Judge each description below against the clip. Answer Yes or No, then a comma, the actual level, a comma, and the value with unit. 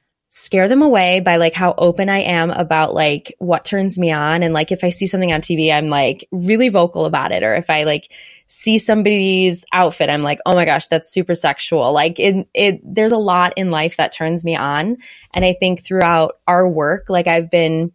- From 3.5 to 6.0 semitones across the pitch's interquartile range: No, narrow, 2.6 semitones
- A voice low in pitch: No, medium, 175 Hz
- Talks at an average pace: No, fast, 220 wpm